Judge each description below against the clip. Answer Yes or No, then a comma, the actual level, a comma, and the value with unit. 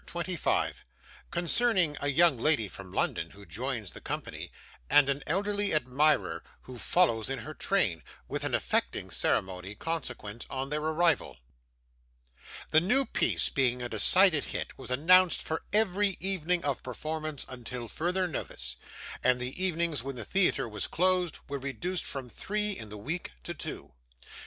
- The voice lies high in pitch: No, medium, 150 Hz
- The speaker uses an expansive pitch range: Yes, wide, 6.4 semitones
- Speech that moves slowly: No, average, 155 wpm